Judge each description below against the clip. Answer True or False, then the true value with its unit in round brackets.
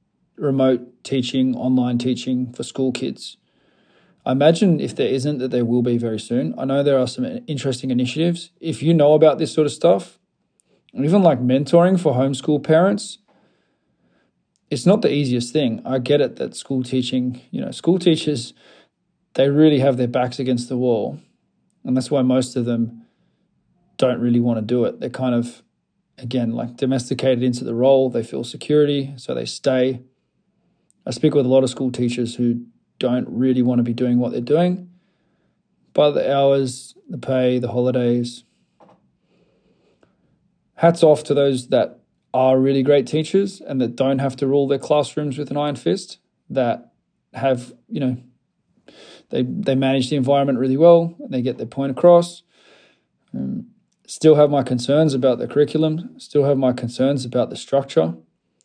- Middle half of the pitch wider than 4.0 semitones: False (2.8 semitones)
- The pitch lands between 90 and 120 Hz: False (130 Hz)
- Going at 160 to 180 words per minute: True (170 wpm)